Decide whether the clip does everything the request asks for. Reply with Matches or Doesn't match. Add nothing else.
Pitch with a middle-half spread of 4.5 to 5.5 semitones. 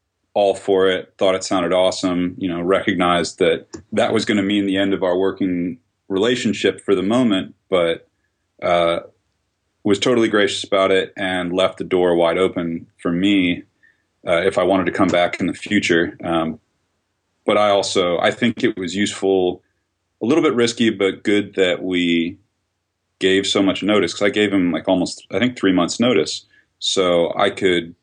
Doesn't match